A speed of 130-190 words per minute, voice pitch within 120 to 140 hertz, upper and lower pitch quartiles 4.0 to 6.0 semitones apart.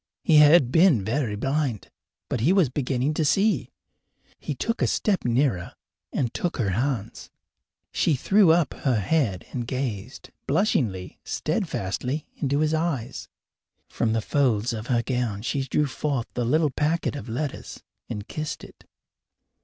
Yes: average, 150 wpm; low, 135 Hz; average, 4.8 semitones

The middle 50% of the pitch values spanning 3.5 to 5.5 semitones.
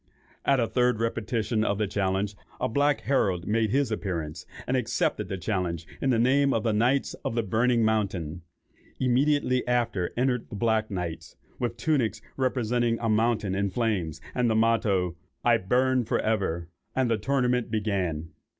Yes: average, 3.8 semitones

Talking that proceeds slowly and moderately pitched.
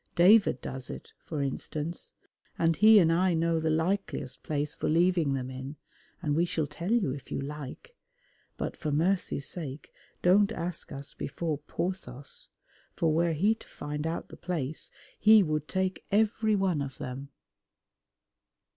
No: average, 155 wpm; medium, 165 Hz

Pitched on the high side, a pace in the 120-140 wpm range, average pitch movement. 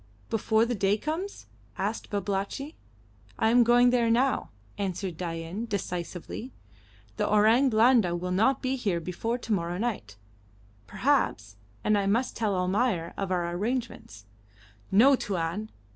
Yes: high, 205 Hz; slow, 135 wpm; average, 4.9 semitones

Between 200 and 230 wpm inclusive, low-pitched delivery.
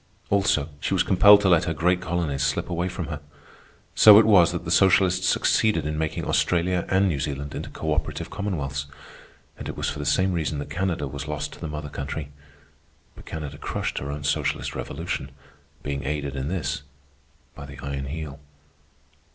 No: average, 185 wpm; very low, 80 Hz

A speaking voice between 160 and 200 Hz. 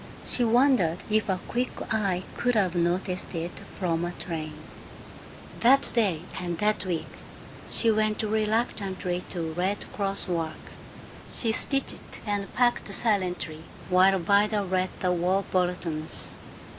Yes: high, 190 Hz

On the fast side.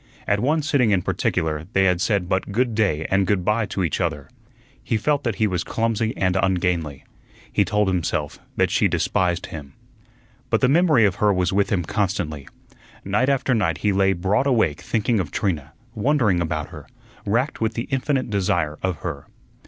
No: average, 185 wpm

